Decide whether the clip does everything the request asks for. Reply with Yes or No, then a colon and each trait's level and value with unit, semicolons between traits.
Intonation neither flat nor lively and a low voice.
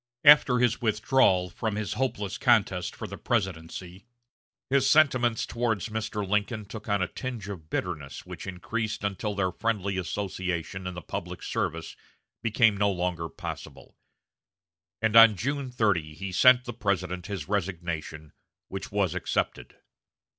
Yes: average, 4.0 semitones; low, 100 Hz